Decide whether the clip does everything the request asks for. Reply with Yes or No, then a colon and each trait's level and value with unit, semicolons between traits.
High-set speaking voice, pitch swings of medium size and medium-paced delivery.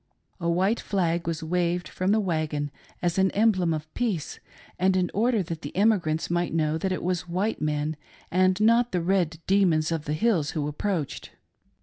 No: medium, 175 Hz; average, 3.4 semitones; average, 185 wpm